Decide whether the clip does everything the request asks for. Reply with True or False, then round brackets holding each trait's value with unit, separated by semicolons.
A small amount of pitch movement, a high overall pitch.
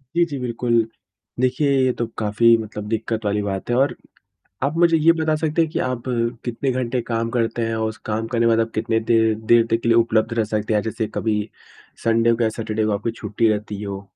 False (2.0 semitones; 115 Hz)